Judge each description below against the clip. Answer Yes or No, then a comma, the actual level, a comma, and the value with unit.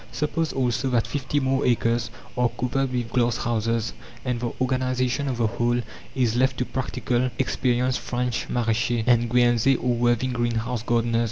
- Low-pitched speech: Yes, low, 120 Hz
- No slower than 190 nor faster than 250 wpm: No, average, 160 wpm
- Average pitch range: No, narrow, 1.5 semitones